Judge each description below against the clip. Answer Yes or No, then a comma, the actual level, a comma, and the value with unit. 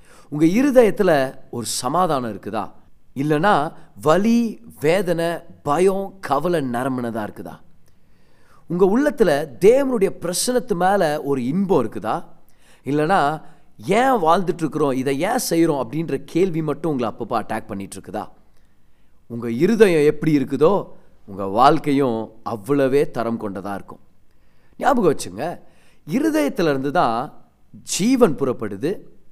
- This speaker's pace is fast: No, average, 105 wpm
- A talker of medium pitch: Yes, medium, 145 Hz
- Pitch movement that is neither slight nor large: No, wide, 7.8 semitones